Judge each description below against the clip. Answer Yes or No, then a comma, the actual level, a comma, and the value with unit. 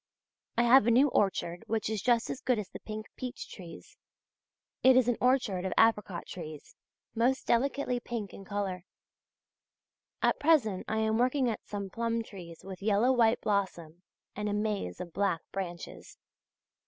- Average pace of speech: Yes, average, 165 wpm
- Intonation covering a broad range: No, average, 4.0 semitones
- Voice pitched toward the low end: No, high, 215 Hz